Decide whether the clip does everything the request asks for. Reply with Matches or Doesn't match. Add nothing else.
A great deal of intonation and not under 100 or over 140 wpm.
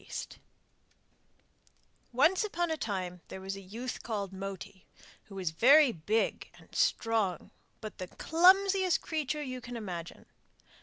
Matches